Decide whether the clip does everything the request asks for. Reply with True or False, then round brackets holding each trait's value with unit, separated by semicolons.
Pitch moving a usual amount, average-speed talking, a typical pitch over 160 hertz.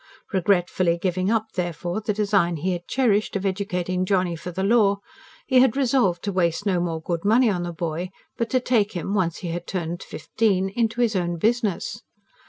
True (3.7 semitones; 190 wpm; 190 Hz)